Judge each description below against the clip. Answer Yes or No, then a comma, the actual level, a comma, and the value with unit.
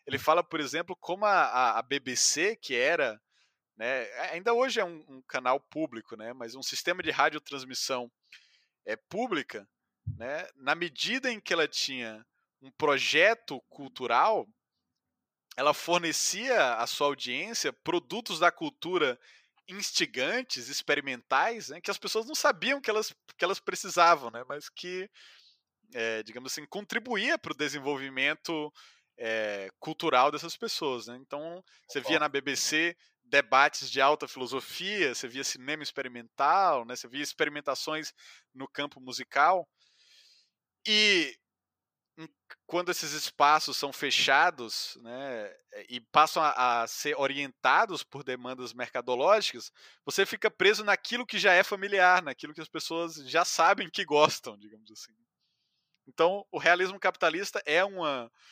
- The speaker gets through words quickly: No, average, 135 wpm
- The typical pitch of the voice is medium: Yes, medium, 155 Hz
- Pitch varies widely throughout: Yes, wide, 6.7 semitones